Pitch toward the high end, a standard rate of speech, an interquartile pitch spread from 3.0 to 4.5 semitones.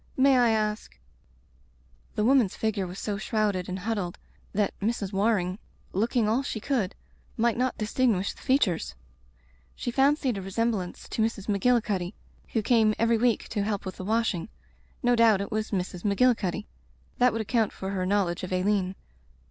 Yes: high, 210 Hz; average, 175 wpm; average, 3.5 semitones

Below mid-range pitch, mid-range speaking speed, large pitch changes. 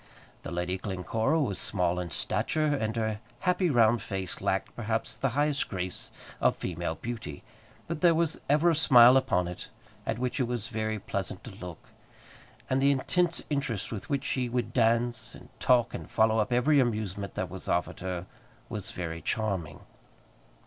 Yes: low, 115 Hz; average, 170 wpm; wide, 5.9 semitones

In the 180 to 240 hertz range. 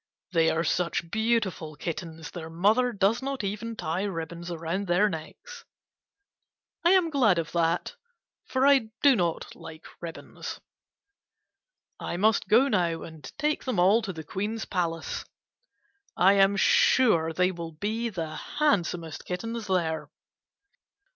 Yes: medium, 185 Hz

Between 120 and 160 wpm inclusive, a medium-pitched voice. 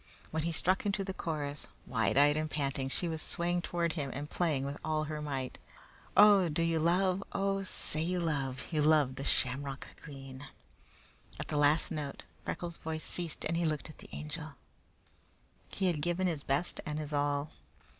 No: average, 185 wpm; medium, 155 Hz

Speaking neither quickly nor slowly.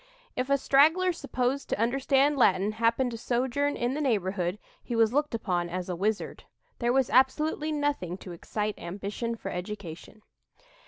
Yes: average, 160 wpm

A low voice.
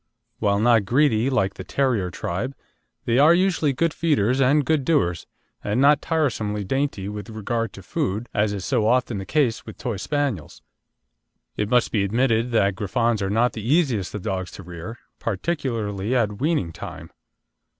Yes: low, 115 Hz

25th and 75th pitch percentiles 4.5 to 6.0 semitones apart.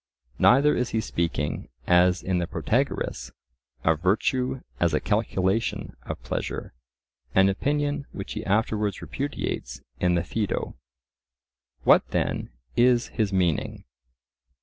Yes: wide, 5.4 semitones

